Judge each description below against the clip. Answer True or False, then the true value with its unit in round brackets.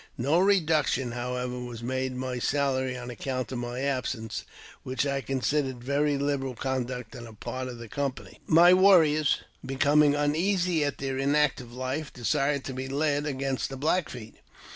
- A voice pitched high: False (135 Hz)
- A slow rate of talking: False (165 wpm)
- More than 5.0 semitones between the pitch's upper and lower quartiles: False (2.7 semitones)